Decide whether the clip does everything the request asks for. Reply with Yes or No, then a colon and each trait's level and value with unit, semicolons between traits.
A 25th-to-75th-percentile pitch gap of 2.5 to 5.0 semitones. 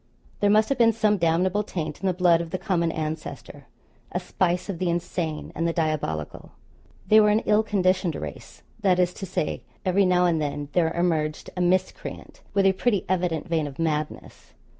Yes: average, 3.0 semitones